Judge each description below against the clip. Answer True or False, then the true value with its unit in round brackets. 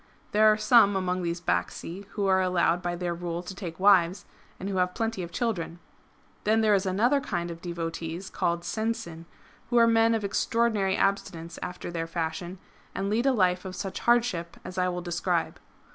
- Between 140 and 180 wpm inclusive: False (190 wpm)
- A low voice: False (185 Hz)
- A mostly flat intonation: False (3.6 semitones)